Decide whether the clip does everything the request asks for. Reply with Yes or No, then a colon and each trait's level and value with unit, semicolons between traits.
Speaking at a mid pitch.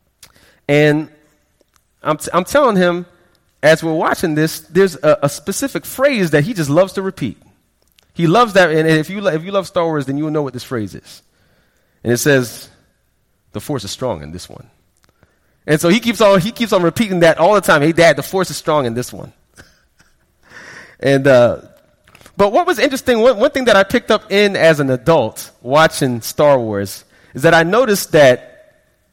Yes: medium, 165 Hz